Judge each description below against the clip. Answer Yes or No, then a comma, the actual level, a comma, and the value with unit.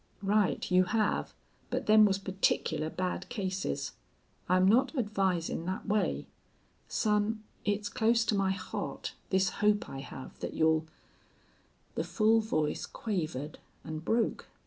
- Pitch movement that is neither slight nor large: Yes, average, 3.0 semitones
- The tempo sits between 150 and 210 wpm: No, slow, 135 wpm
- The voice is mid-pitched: No, high, 195 Hz